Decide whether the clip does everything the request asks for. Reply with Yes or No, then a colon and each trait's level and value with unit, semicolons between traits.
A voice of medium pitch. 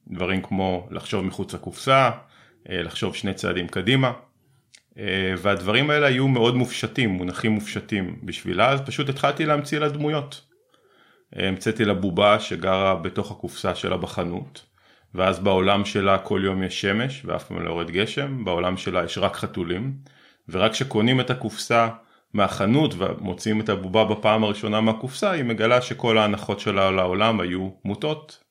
No: low, 110 Hz